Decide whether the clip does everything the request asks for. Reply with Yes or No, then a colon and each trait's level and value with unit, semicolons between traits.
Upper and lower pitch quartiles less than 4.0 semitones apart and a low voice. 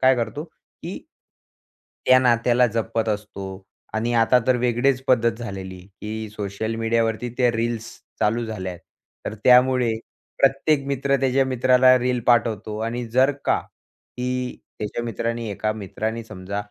Yes: narrow, 2.5 semitones; low, 115 Hz